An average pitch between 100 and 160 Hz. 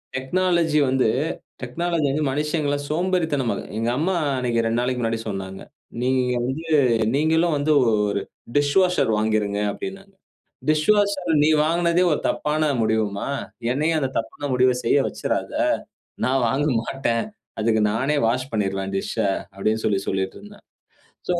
Yes: low, 135 Hz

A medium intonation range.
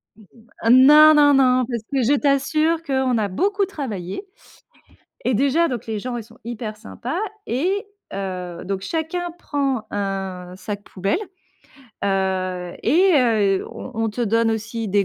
No: wide, 6.3 semitones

